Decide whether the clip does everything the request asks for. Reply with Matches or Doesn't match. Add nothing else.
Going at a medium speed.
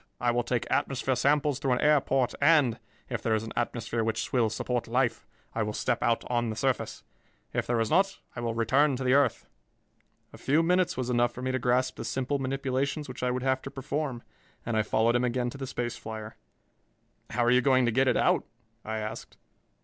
Doesn't match